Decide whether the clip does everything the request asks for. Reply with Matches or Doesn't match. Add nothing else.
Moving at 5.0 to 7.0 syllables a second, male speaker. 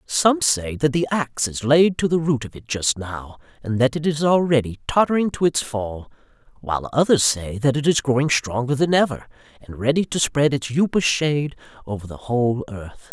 Matches